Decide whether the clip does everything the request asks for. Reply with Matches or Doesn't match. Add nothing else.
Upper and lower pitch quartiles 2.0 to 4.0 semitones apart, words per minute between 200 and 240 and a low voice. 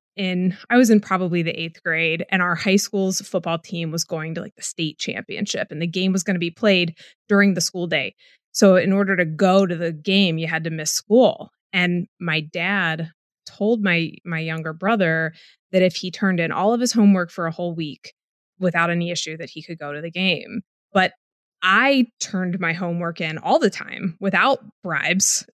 Doesn't match